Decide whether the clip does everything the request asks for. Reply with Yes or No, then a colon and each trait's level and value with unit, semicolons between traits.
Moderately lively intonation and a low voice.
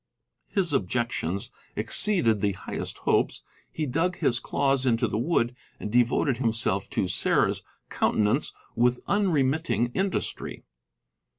No: wide, 5.8 semitones; low, 125 Hz